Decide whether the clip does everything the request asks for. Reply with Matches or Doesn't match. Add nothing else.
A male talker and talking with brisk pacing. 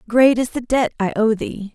Doesn't match